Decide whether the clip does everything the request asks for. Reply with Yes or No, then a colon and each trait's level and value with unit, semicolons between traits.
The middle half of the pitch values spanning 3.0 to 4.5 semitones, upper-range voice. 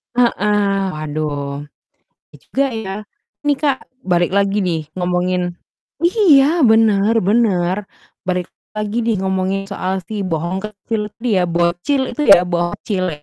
Yes: average, 3.9 semitones; high, 195 Hz